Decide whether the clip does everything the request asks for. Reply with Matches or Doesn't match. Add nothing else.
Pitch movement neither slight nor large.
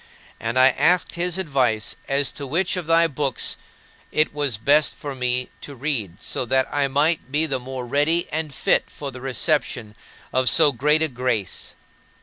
Matches